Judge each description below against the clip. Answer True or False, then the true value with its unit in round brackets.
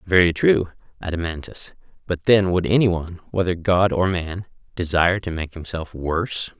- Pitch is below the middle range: True (90 Hz)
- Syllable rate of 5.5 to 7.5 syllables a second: False (5.1 syllables/s)